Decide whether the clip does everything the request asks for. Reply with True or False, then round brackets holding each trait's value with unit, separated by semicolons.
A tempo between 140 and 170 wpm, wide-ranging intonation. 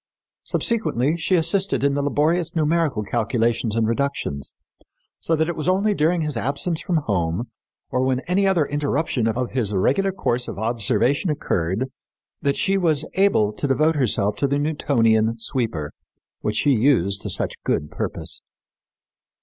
True (155 wpm; 6.1 semitones)